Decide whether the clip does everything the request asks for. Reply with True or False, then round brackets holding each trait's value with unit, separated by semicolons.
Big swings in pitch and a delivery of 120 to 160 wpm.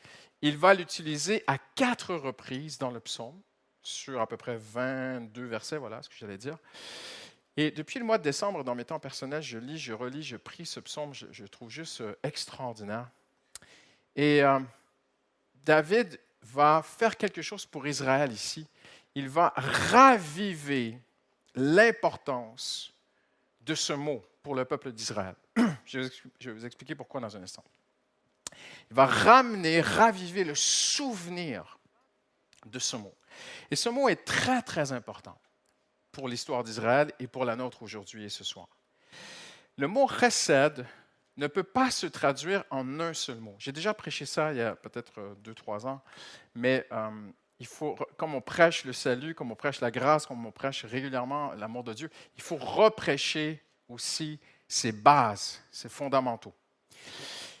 False (4.8 semitones; 155 wpm)